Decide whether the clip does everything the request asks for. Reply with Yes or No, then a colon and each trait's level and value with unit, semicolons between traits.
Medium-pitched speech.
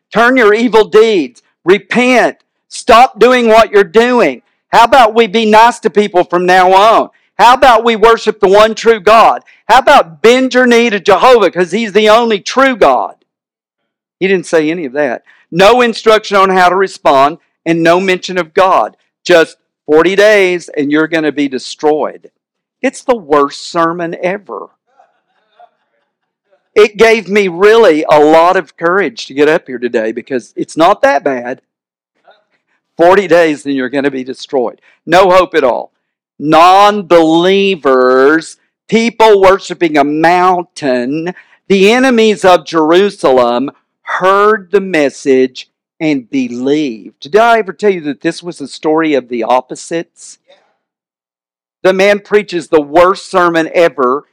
Yes: medium, 180 Hz